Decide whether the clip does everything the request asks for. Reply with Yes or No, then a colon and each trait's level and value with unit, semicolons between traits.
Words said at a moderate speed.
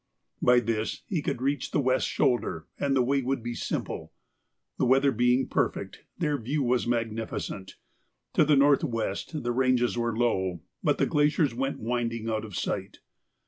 Yes: average, 170 wpm